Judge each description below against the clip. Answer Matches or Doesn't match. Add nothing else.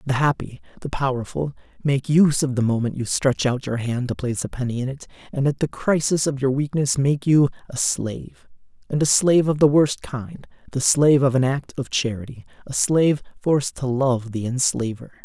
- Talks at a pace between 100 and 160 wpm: Doesn't match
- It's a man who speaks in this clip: Matches